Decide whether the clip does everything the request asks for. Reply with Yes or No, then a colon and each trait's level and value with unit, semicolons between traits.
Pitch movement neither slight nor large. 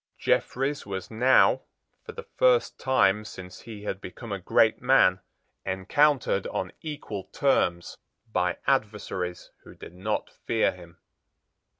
No: wide, 6.1 semitones